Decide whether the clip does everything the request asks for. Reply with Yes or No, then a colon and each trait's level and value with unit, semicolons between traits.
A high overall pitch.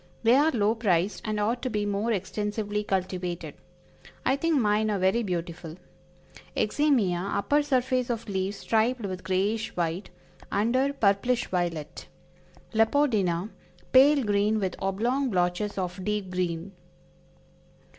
Yes: high, 210 Hz